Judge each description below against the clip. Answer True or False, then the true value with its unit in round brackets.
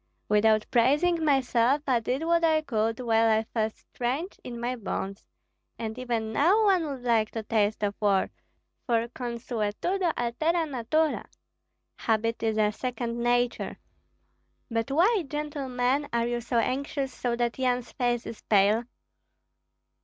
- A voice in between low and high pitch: False (240 Hz)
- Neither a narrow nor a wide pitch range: True (3.9 semitones)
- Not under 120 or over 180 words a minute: True (140 wpm)